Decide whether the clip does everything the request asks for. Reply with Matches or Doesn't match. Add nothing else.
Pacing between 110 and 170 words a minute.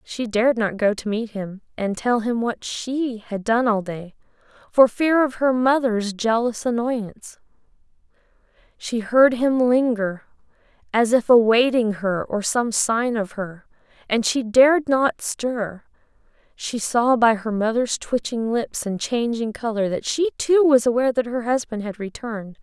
Matches